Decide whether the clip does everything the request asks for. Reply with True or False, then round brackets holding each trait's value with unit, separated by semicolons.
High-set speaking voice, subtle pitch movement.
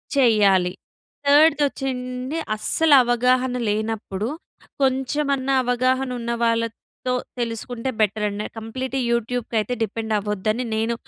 False (240 Hz; 3.0 semitones)